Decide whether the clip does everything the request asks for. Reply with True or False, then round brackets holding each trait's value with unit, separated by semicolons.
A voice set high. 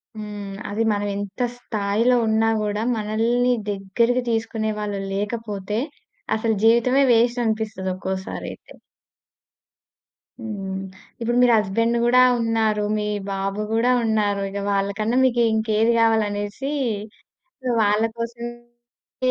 True (220 Hz)